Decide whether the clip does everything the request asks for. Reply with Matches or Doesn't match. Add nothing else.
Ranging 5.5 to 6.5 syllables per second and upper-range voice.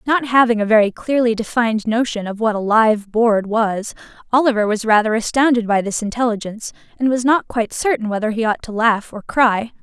Matches